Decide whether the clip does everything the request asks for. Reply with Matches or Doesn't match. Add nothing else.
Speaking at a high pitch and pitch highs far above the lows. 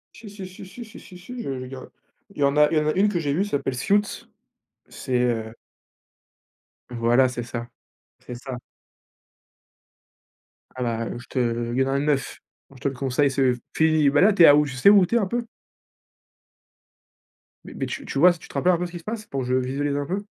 Doesn't match